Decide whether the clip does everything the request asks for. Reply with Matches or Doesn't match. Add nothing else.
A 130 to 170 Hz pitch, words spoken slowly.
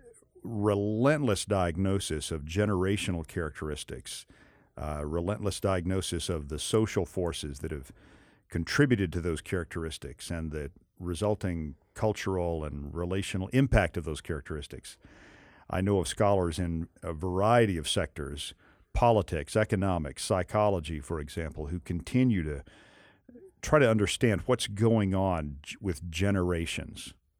Doesn't match